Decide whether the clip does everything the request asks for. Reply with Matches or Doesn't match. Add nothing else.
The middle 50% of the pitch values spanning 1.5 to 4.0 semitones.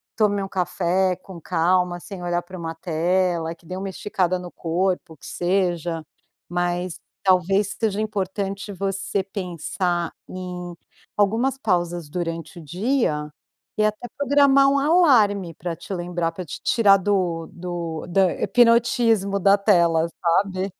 Matches